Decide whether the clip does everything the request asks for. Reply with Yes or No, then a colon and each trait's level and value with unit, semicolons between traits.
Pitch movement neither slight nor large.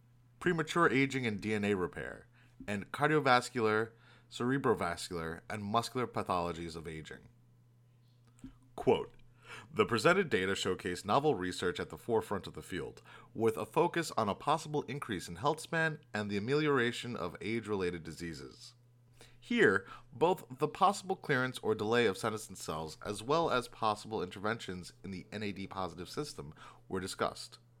Yes: average, 3.5 semitones